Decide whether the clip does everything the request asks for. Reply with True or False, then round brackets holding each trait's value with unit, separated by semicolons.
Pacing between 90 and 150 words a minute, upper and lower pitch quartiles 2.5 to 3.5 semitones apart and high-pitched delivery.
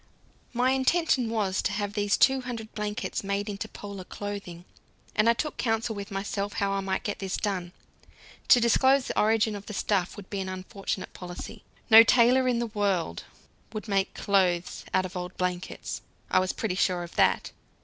False (185 wpm; 3.0 semitones; 205 Hz)